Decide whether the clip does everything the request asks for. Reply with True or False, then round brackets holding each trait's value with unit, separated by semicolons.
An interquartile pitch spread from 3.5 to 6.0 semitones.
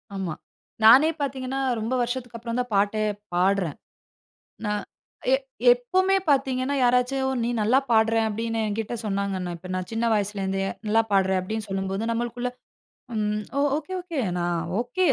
True (4.0 semitones)